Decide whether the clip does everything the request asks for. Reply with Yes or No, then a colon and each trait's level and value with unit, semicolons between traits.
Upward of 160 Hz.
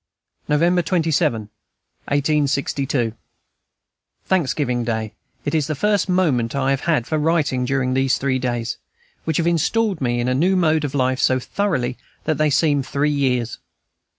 No: medium, 140 Hz